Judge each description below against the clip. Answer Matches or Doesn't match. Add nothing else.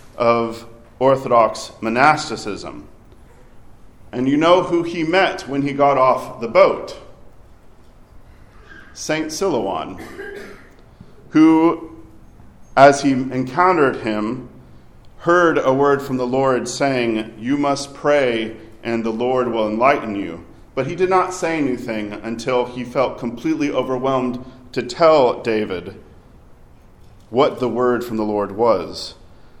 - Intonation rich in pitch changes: Doesn't match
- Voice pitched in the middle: Doesn't match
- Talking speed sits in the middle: Doesn't match